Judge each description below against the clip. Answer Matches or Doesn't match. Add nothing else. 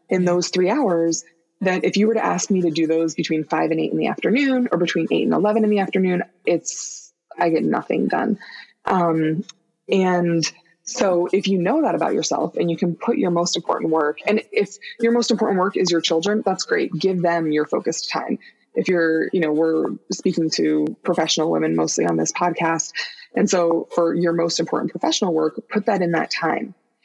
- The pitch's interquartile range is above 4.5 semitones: Doesn't match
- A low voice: Doesn't match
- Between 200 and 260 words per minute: Matches